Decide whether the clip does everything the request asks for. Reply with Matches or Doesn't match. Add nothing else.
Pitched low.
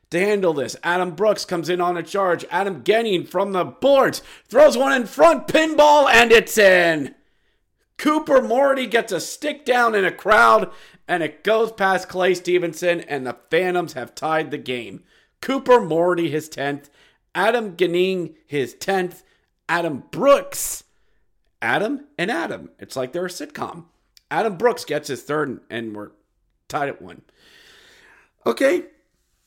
Doesn't match